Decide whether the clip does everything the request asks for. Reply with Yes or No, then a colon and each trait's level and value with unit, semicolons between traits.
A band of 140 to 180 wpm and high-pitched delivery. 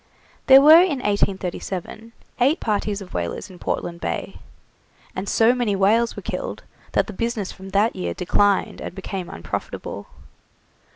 Yes: average, 150 wpm; high, 205 Hz